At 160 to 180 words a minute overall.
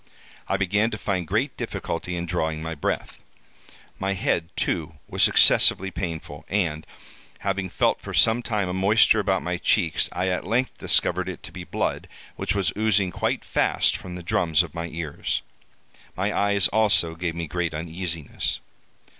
Yes: average, 165 wpm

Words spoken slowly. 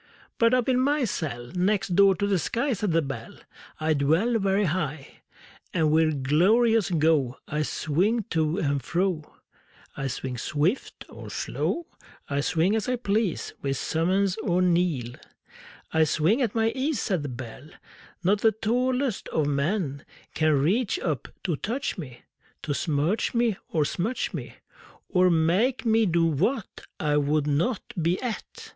No: average, 155 wpm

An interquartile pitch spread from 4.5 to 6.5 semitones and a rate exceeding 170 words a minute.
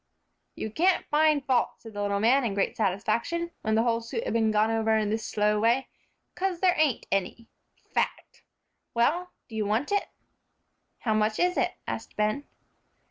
Yes: wide, 5.6 semitones; average, 180 wpm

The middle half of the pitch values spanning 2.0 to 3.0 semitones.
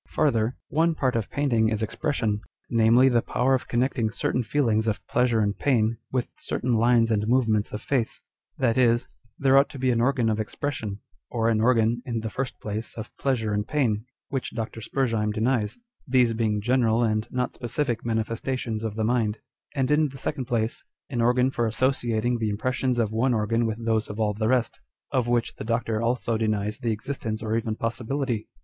Yes: narrow, 2.6 semitones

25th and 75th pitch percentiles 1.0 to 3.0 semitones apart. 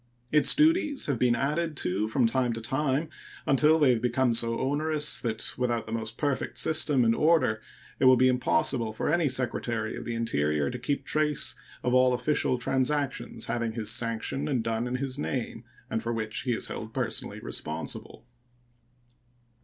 No: average, 3.8 semitones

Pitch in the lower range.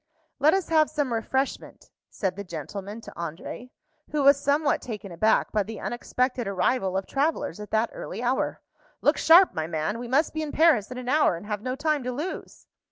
No: high, 245 Hz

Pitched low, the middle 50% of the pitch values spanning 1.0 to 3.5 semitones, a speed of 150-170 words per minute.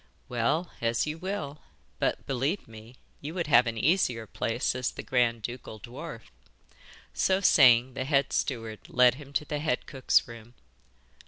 No: low, 125 Hz; average, 4.2 semitones; average, 160 wpm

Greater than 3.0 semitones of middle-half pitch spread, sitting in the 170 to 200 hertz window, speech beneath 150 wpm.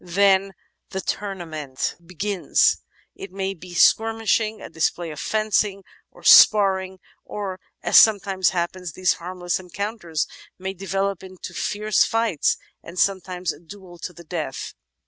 No: narrow, 2.4 semitones; high, 190 Hz; slow, 135 wpm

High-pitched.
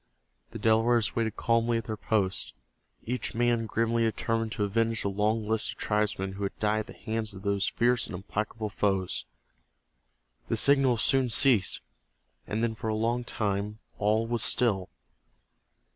No: low, 110 Hz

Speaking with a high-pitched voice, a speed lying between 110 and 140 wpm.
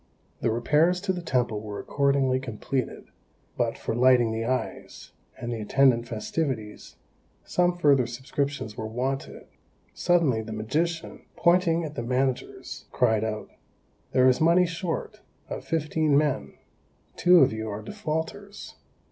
No: low, 135 Hz; slow, 135 wpm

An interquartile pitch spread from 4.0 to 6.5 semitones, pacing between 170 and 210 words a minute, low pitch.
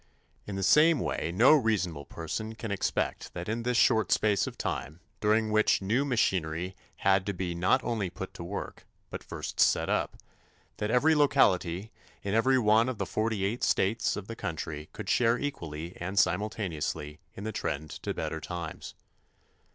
Yes: average, 4.4 semitones; average, 175 wpm; low, 100 Hz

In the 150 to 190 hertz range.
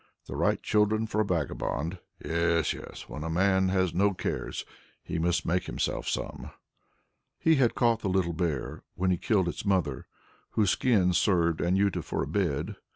No: very low, 90 Hz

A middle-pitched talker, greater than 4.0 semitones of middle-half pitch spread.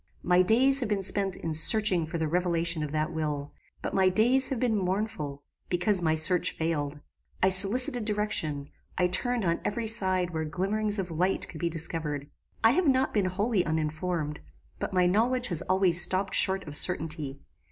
Yes: medium, 180 Hz; average, 4.7 semitones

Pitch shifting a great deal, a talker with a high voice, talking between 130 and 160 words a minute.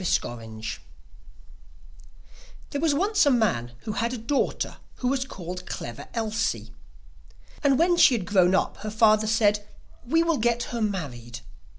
Yes: wide, 6.3 semitones; high, 220 Hz; average, 155 wpm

